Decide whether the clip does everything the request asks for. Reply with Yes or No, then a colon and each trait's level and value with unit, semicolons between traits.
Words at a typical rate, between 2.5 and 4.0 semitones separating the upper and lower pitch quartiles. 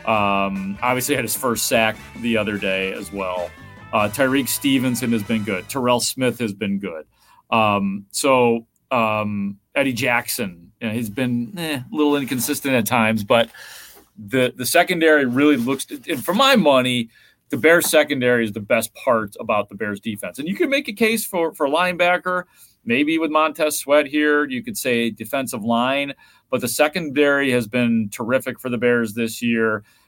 No: average, 180 wpm; average, 5.0 semitones